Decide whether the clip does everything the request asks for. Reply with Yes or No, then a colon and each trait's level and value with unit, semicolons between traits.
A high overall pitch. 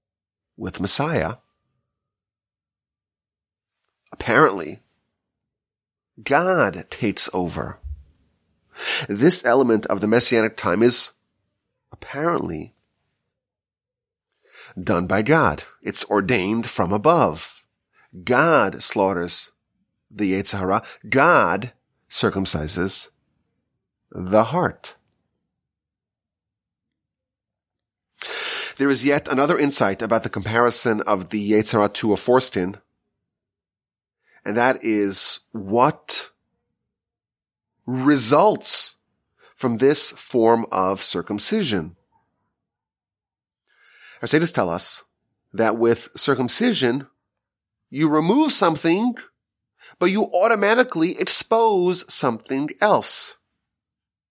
No: low, 115 Hz